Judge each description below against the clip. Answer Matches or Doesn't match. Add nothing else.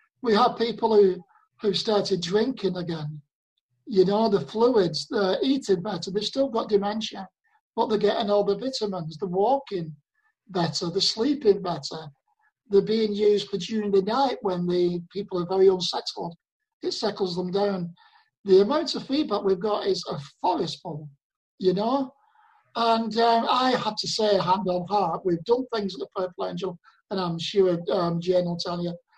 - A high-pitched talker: Matches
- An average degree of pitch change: Matches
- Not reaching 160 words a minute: Doesn't match